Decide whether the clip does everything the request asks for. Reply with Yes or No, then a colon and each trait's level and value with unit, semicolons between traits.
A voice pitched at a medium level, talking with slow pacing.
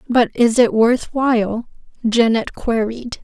No: high, 235 Hz; slow, 130 wpm